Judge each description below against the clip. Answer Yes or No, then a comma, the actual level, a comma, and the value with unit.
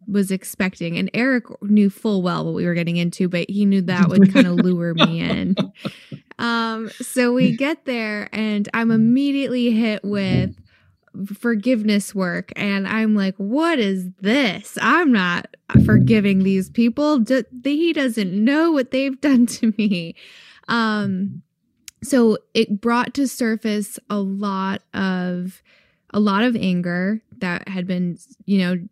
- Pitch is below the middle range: No, high, 210 Hz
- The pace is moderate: Yes, average, 145 wpm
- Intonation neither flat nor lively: Yes, average, 3.8 semitones